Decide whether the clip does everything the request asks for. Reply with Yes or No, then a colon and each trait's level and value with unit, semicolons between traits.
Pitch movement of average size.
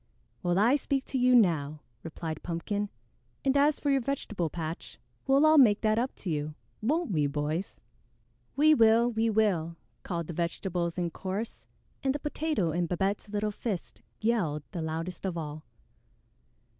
No: wide, 6.5 semitones